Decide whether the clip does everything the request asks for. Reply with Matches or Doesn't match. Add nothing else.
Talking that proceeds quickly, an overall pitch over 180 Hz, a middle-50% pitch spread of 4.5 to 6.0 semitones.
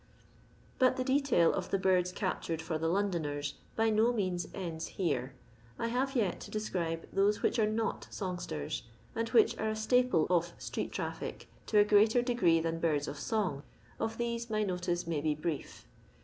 Doesn't match